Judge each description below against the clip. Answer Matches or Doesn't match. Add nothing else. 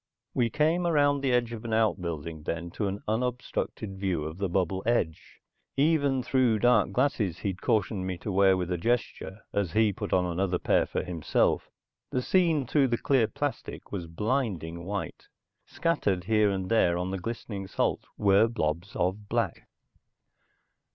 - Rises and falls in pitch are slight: Doesn't match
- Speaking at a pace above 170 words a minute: Doesn't match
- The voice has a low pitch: Matches